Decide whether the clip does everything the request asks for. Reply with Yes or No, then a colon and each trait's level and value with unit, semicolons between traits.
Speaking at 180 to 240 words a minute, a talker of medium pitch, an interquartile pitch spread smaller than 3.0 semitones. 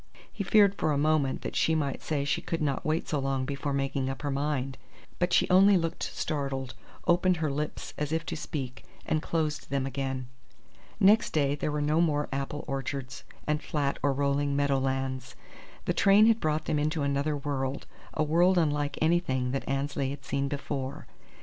Yes: average, 190 wpm; medium, 145 Hz; narrow, 2.4 semitones